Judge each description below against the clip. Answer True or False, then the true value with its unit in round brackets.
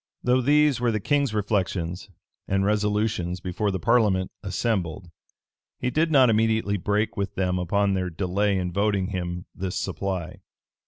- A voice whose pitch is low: True (100 Hz)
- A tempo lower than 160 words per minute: True (150 wpm)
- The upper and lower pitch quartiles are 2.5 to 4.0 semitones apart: True (3.3 semitones)